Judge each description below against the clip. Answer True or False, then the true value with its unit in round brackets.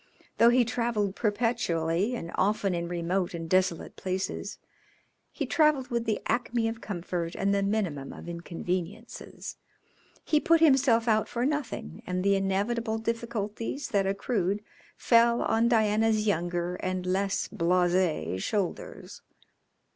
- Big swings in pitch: False (4.4 semitones)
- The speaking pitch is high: True (205 Hz)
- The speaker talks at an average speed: False (130 wpm)